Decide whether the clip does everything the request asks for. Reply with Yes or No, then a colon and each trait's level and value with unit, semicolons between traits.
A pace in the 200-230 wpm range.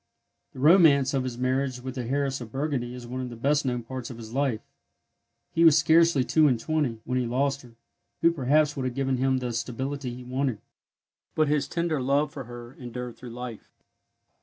Yes: fast, 205 wpm